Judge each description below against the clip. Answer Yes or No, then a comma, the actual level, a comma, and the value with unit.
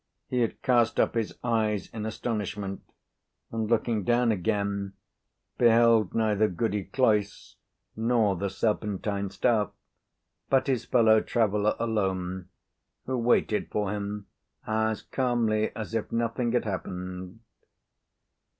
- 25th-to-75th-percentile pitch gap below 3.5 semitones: Yes, narrow, 2.4 semitones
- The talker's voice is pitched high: No, low, 110 Hz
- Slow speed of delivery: Yes, slow, 115 wpm